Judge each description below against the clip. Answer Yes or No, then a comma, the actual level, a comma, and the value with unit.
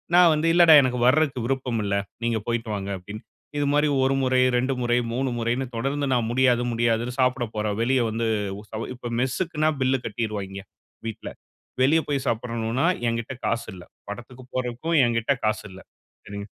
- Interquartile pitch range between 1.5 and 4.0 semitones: Yes, average, 2.8 semitones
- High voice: No, low, 120 Hz